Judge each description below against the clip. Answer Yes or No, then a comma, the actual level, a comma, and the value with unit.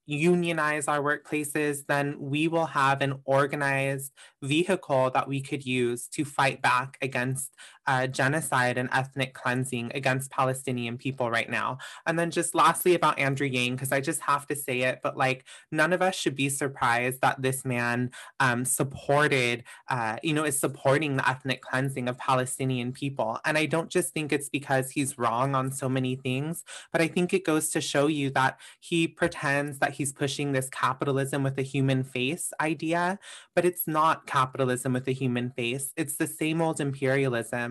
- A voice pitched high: No, medium, 140 Hz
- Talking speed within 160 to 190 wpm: Yes, average, 180 wpm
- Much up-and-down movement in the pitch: No, average, 2.8 semitones